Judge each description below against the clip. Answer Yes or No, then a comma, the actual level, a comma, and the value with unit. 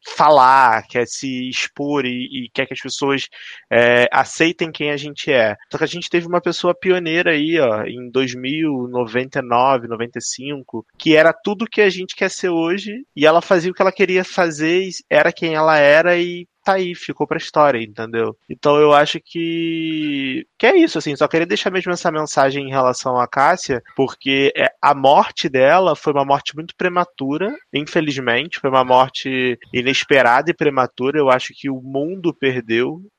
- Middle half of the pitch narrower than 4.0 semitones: No, average, 4.9 semitones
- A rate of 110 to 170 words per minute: No, average, 180 wpm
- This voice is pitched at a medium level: Yes, medium, 150 Hz